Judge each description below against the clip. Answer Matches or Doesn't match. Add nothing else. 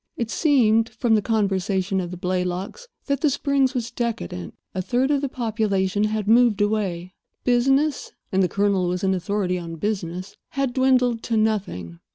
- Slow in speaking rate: Doesn't match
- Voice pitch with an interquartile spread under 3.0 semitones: Doesn't match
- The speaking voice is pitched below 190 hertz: Doesn't match